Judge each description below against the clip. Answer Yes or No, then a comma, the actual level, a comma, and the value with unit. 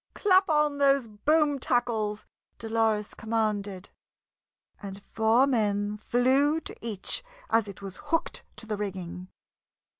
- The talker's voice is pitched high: Yes, high, 220 Hz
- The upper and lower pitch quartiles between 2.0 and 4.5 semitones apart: No, average, 5.0 semitones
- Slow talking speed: Yes, slow, 120 wpm